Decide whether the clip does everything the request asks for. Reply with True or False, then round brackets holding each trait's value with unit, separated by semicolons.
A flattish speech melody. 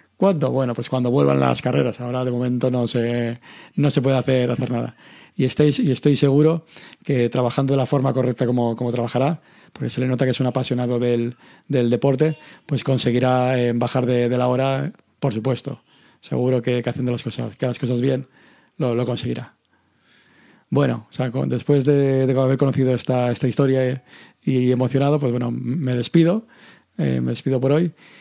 True (2.1 semitones)